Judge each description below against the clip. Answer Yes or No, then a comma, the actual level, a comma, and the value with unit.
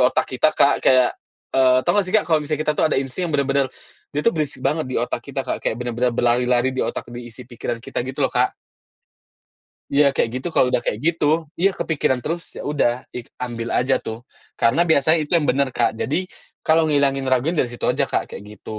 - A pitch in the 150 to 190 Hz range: No, low, 135 Hz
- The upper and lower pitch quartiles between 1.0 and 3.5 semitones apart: No, average, 4.0 semitones